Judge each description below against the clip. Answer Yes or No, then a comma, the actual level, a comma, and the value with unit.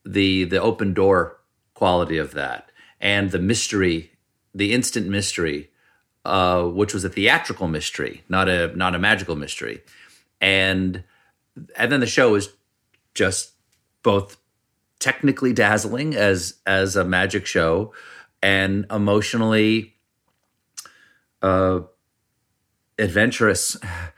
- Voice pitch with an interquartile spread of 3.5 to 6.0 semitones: No, average, 2.9 semitones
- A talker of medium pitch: No, low, 100 Hz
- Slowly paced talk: Yes, slow, 110 wpm